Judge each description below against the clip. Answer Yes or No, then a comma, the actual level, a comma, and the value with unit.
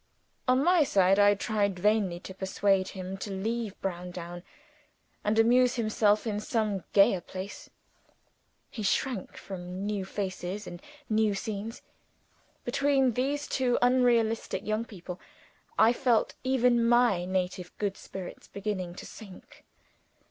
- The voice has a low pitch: No, high, 210 Hz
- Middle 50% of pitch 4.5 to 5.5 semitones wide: No, average, 3.8 semitones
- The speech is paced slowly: Yes, slow, 125 wpm